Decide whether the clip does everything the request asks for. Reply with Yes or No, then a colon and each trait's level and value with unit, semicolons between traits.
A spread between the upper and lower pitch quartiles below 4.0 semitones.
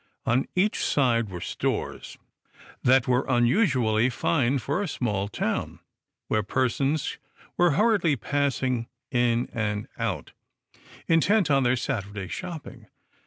No: average, 4.3 semitones